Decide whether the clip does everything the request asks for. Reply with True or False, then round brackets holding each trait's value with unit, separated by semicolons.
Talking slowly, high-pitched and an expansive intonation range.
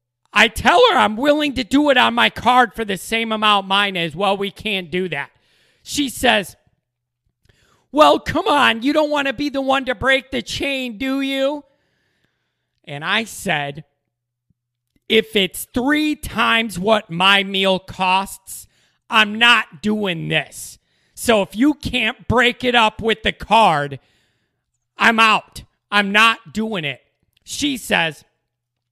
False (150 wpm; 210 Hz; 7.5 semitones)